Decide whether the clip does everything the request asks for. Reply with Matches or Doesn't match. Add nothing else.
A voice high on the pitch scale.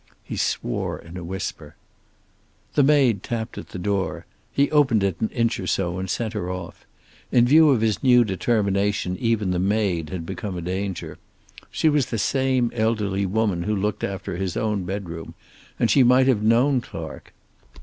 Doesn't match